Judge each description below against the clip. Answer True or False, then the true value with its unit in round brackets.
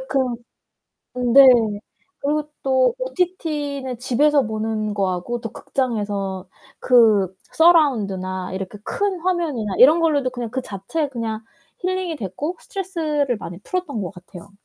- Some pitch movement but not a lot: False (6.7 semitones)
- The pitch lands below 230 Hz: False (255 Hz)